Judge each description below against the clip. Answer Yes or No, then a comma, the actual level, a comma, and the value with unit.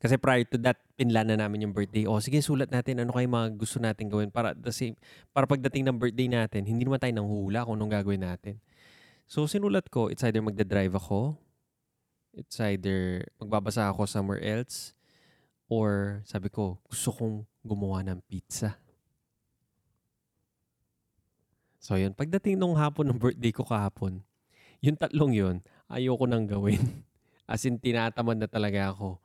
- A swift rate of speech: Yes, fast, 160 wpm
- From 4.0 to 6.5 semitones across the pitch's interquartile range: No, average, 3.6 semitones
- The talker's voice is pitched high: No, low, 110 Hz